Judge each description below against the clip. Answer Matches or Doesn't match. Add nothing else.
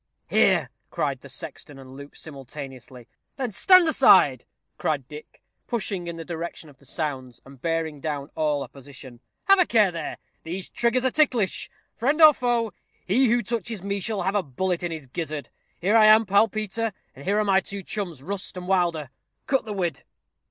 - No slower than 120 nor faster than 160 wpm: Doesn't match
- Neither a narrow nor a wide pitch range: Doesn't match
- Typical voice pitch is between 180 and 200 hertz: Matches